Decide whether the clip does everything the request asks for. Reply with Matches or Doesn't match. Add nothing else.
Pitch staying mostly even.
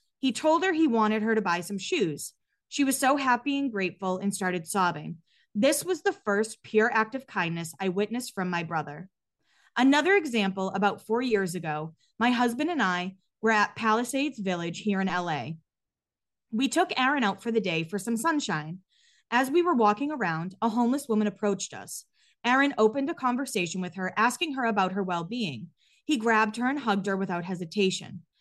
Doesn't match